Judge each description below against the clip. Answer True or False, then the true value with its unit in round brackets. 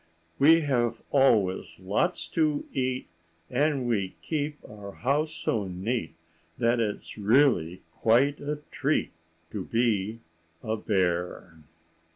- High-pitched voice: False (115 Hz)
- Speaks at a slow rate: True (115 wpm)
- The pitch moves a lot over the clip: True (6.1 semitones)